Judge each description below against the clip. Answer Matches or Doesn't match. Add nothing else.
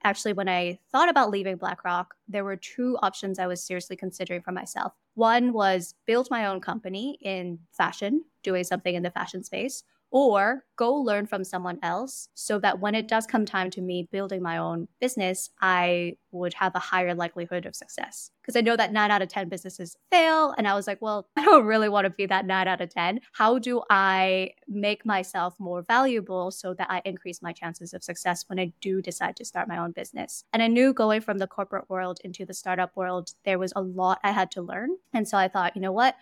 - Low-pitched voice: Doesn't match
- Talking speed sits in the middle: Doesn't match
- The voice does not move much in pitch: Doesn't match